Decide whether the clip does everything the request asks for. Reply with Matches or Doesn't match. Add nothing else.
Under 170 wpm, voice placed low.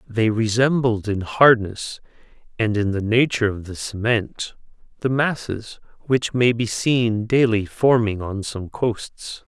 Matches